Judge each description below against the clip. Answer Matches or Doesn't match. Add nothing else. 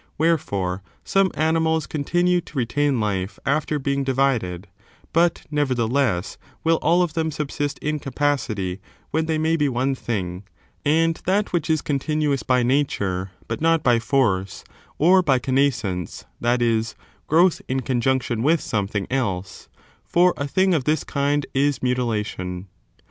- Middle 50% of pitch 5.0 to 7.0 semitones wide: Matches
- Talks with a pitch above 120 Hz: Matches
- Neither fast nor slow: Matches